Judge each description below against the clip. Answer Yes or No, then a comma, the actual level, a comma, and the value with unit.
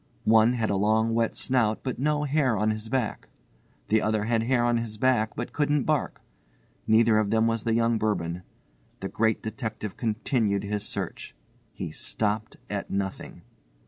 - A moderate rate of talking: Yes, average, 170 wpm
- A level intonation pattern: Yes, narrow, 2.0 semitones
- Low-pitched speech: Yes, low, 110 Hz